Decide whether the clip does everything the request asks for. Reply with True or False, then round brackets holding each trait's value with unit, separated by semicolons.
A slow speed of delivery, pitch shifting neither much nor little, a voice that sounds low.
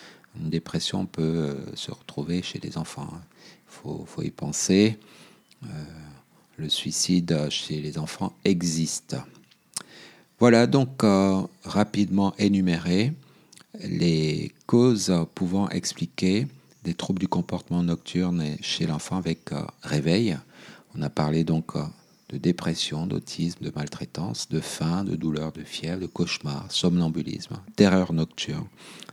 True (115 wpm; 4.0 semitones; 85 Hz)